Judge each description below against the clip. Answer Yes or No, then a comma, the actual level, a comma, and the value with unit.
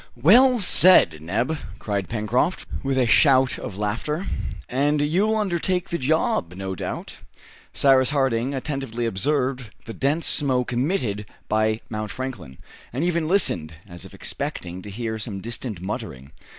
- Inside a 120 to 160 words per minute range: Yes, average, 140 wpm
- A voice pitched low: Yes, low, 125 Hz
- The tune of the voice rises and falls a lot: Yes, wide, 6.2 semitones